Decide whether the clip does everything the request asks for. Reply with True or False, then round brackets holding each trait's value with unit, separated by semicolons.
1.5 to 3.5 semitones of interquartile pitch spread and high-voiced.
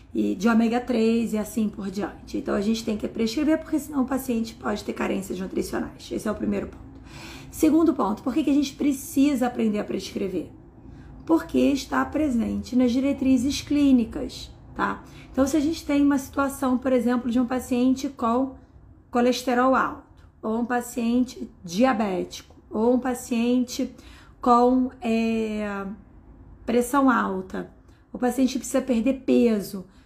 True (2.9 semitones; 250 Hz)